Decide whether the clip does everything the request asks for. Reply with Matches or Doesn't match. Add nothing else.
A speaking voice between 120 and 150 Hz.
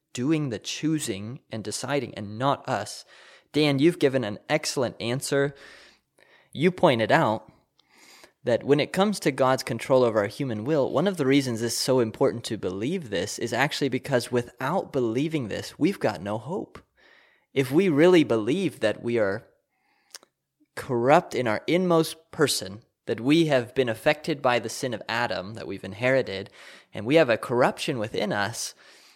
Matches